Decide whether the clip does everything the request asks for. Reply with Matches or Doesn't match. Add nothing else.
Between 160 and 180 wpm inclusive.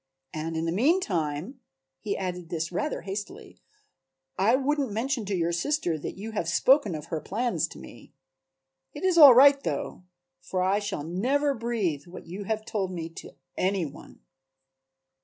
Matches